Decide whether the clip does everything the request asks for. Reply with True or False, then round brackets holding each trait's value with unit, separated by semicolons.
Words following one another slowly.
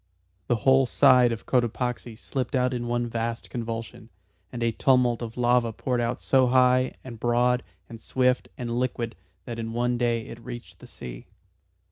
False (170 wpm)